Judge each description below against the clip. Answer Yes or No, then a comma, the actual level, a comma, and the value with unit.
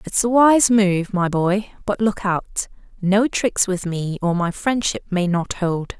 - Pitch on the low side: No, high, 195 Hz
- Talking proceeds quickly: No, average, 190 wpm